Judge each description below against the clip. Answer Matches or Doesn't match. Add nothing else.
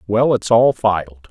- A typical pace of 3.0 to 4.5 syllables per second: Matches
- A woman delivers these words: Doesn't match